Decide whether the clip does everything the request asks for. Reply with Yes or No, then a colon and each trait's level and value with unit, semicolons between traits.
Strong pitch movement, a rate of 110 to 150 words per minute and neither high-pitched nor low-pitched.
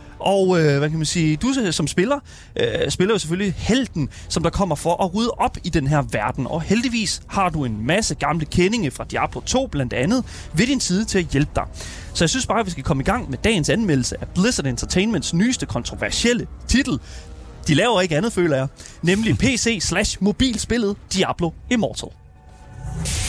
No: wide, 7.3 semitones; average, 190 wpm; medium, 180 Hz